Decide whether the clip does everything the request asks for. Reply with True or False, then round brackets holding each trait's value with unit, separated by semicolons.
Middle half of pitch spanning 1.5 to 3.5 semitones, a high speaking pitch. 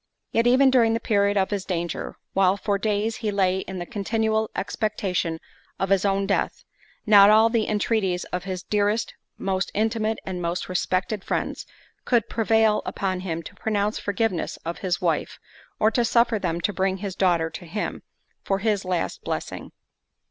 True (2.8 semitones; 200 Hz)